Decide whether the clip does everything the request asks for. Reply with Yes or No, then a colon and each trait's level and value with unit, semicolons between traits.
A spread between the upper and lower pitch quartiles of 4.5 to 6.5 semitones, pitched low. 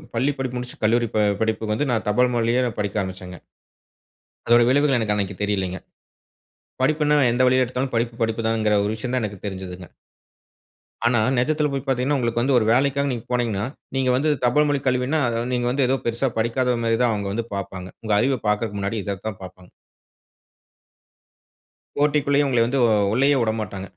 No: average, 3.7 semitones; low, 120 Hz